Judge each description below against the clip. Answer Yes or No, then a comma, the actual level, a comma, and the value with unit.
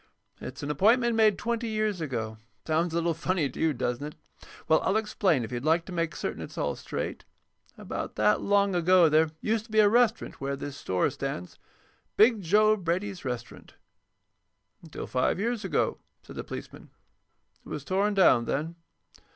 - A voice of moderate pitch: Yes, medium, 170 Hz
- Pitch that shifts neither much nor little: No, wide, 6.7 semitones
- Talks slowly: No, average, 175 wpm